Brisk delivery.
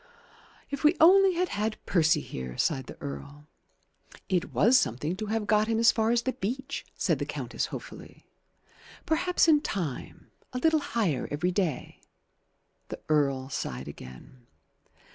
No: average, 155 wpm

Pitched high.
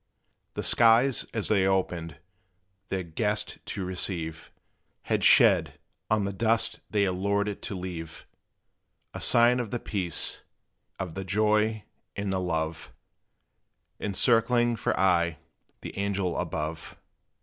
No: low, 100 Hz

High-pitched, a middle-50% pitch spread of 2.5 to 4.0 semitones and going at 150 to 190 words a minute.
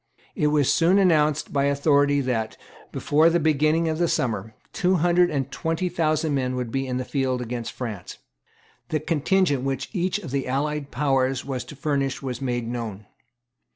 No: medium, 140 Hz; average, 3.7 semitones; average, 170 wpm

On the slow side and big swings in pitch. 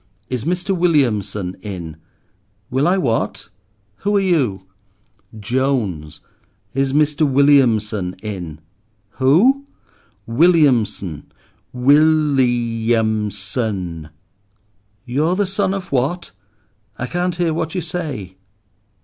Yes: slow, 100 wpm; wide, 7.5 semitones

